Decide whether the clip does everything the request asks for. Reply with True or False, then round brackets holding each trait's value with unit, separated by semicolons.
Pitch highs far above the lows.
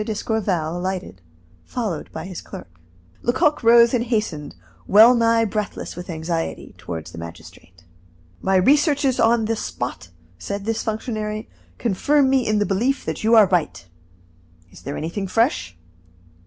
True (5.8 semitones)